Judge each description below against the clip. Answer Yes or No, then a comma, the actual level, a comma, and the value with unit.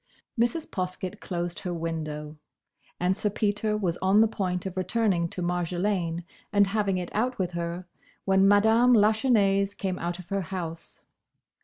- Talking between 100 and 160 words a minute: Yes, average, 155 wpm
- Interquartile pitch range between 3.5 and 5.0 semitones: No, average, 3.0 semitones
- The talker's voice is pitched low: No, high, 190 Hz